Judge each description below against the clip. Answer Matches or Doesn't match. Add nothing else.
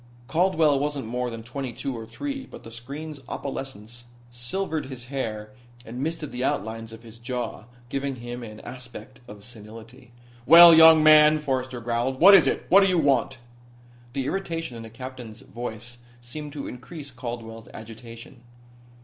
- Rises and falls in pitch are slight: Doesn't match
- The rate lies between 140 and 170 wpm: Matches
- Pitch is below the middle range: Matches